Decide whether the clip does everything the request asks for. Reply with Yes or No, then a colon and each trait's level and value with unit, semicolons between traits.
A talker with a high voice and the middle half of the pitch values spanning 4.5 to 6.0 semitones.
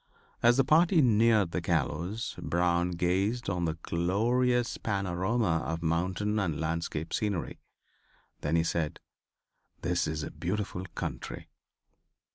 No: very low, 90 Hz; average, 4.8 semitones